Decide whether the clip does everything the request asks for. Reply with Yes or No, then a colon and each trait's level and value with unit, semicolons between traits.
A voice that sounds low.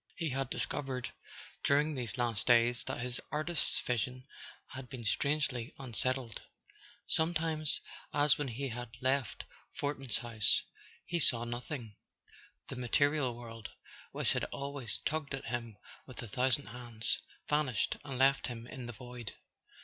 Yes: low, 125 Hz